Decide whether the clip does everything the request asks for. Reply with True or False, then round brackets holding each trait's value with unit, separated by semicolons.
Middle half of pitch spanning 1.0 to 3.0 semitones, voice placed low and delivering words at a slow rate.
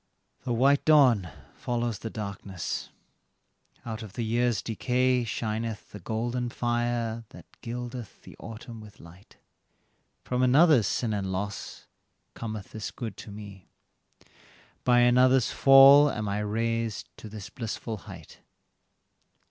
True (2.7 semitones; 115 Hz; 125 wpm)